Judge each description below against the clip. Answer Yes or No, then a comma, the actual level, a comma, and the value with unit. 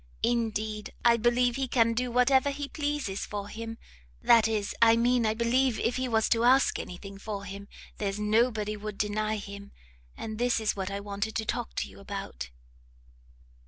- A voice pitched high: Yes, high, 220 Hz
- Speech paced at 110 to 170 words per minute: No, average, 185 wpm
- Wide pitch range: No, average, 2.8 semitones